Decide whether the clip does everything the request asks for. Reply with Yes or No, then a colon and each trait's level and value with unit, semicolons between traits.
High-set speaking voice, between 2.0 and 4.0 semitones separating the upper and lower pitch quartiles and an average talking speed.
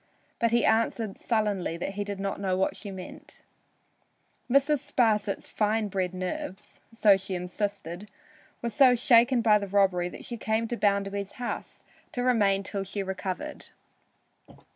Yes: high, 205 Hz; average, 3.0 semitones; average, 150 wpm